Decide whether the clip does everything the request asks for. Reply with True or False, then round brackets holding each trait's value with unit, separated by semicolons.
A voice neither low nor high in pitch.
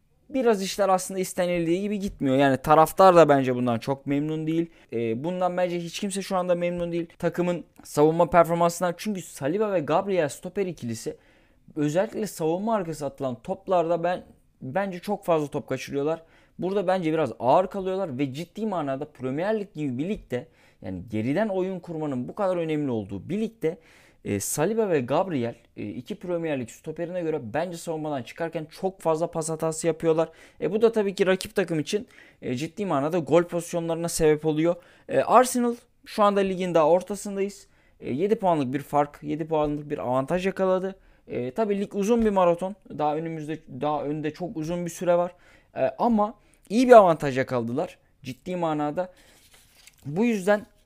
True (170 Hz)